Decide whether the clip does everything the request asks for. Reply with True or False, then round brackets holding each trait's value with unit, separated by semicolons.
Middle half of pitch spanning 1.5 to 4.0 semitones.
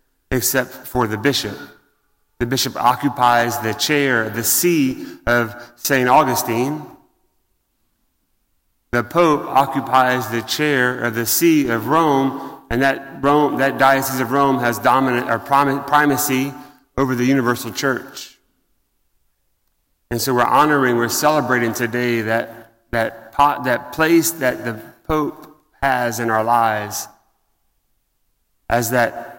True (3.2 semitones)